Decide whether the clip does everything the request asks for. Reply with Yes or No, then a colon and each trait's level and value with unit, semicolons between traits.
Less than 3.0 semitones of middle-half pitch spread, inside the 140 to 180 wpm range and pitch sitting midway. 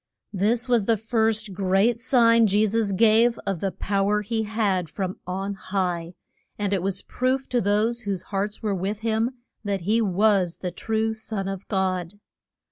No: narrow, 2.6 semitones; average, 175 wpm; high, 205 Hz